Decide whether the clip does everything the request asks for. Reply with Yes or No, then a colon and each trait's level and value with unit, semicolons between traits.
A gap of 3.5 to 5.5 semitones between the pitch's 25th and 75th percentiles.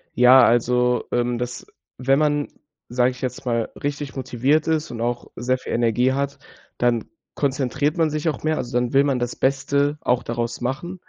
No: average, 2.7 semitones